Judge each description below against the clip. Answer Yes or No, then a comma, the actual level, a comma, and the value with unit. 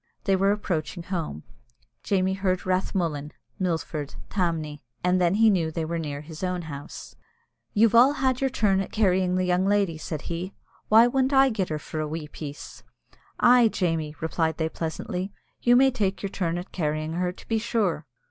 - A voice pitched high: No, medium, 180 Hz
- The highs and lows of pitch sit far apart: No, average, 4.1 semitones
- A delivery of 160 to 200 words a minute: Yes, average, 185 wpm